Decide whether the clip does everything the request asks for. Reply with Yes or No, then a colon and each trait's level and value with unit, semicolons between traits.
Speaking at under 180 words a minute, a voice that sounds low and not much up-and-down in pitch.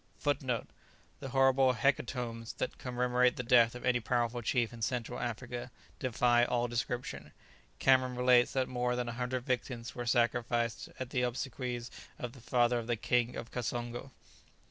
Yes: average, 165 wpm; low, 125 Hz; narrow, 1.0 semitones